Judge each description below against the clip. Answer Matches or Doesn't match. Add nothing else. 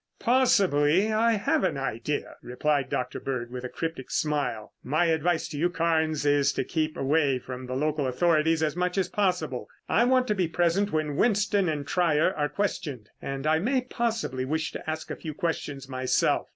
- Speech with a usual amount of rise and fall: Matches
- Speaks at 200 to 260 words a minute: Doesn't match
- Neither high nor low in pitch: Matches